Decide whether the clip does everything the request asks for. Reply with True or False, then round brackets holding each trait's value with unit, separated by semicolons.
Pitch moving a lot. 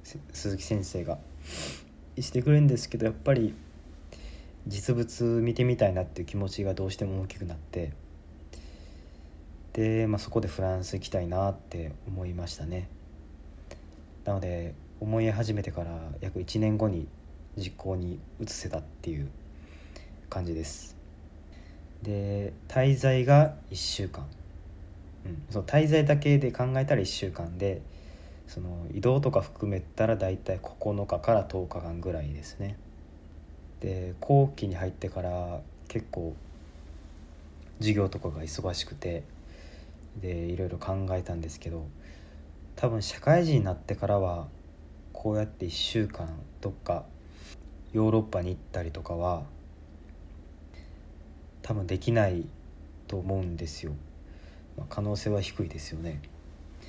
False (4.6 semitones)